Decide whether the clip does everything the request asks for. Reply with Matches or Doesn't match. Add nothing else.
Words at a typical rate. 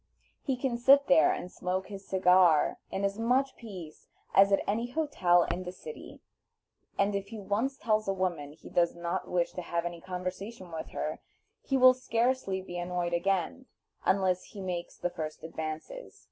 Matches